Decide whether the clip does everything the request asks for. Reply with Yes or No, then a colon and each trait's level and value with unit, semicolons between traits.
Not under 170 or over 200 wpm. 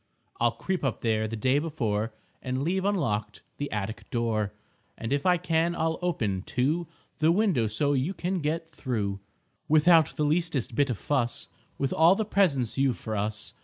Yes: average, 175 wpm